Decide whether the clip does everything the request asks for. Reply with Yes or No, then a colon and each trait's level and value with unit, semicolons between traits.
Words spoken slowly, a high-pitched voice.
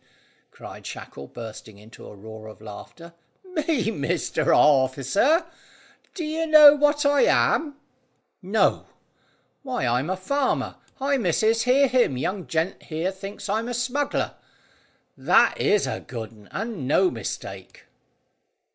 Yes: slow, 130 wpm; high, 205 Hz